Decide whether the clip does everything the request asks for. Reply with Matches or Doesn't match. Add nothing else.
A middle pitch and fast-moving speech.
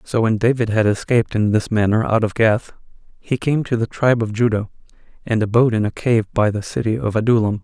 Doesn't match